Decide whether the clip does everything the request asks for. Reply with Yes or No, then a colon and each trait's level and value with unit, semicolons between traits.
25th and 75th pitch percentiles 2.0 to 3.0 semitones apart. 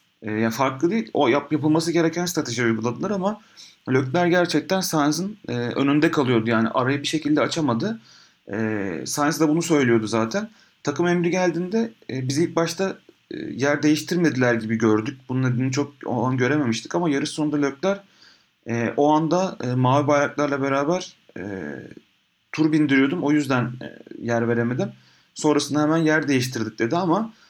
No: wide, 5.5 semitones